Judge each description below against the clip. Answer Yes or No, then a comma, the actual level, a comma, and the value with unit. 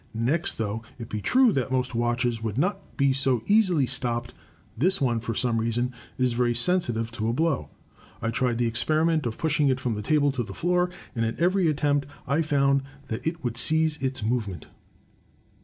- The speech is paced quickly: No, average, 190 wpm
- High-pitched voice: No, low, 130 Hz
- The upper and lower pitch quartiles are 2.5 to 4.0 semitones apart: No, average, 4.9 semitones